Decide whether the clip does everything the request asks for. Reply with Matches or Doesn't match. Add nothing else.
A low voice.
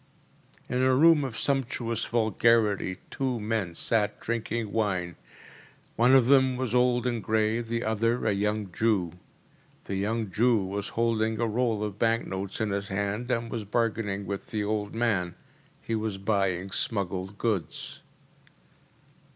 Matches